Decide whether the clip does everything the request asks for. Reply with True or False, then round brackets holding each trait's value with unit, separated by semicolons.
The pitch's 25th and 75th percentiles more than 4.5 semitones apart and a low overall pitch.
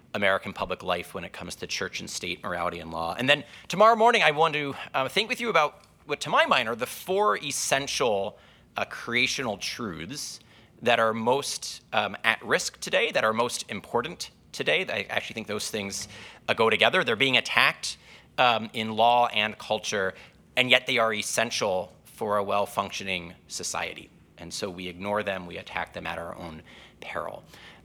True (5.0 semitones; 110 Hz)